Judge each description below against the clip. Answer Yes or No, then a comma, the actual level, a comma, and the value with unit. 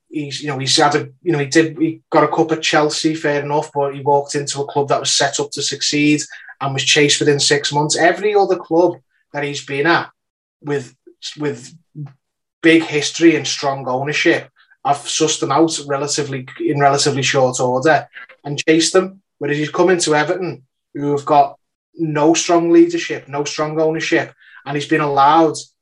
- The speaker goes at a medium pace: Yes, average, 190 wpm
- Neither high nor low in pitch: Yes, medium, 150 Hz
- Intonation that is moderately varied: No, narrow, 2.1 semitones